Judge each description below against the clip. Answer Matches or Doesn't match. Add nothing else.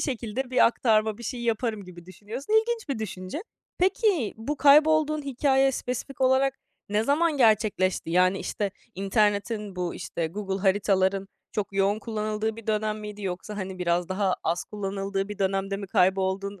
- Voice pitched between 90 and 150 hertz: Doesn't match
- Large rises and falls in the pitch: Doesn't match